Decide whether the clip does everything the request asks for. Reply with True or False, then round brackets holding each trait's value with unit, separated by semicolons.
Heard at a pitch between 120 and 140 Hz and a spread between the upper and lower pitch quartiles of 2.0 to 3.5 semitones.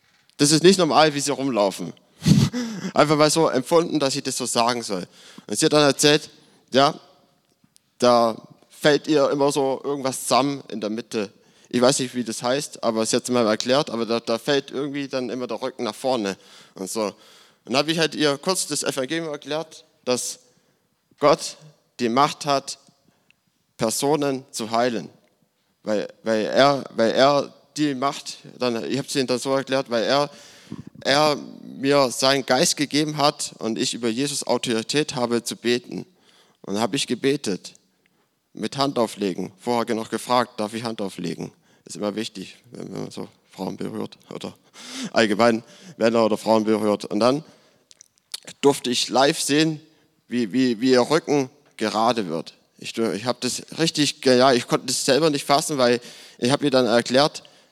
False (135 Hz; 3.9 semitones)